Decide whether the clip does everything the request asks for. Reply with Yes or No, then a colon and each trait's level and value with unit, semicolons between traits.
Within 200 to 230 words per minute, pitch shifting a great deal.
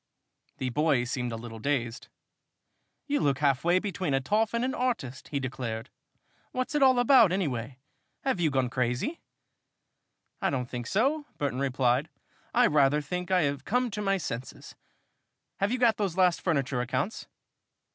No: average, 165 wpm; wide, 8.4 semitones